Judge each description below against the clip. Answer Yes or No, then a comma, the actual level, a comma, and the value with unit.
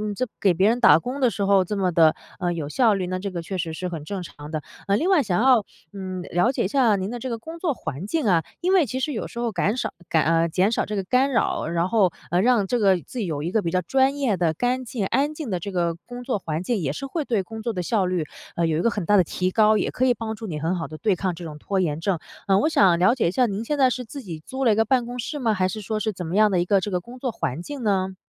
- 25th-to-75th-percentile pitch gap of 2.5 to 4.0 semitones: No, wide, 5.6 semitones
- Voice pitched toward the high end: Yes, high, 200 Hz